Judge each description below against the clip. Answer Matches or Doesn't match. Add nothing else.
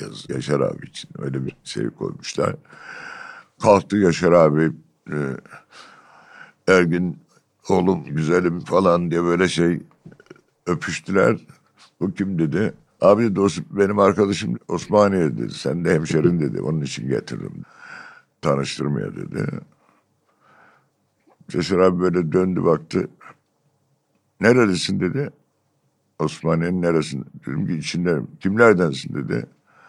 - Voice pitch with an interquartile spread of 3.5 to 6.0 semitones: Matches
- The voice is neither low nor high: Doesn't match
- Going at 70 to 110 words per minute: Matches